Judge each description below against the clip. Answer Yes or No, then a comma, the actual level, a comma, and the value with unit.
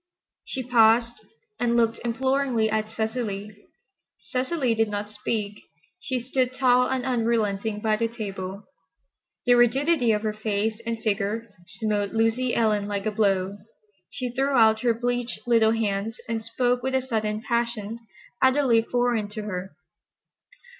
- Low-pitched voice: No, high, 225 Hz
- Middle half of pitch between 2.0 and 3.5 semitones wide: Yes, narrow, 2.5 semitones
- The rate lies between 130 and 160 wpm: Yes, average, 140 wpm